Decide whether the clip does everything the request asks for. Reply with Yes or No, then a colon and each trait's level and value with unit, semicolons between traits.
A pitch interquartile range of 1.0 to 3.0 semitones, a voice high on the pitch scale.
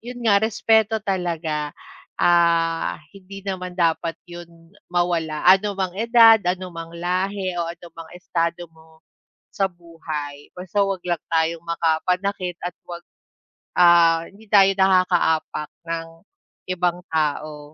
No: narrow, 2.6 semitones; medium, 175 Hz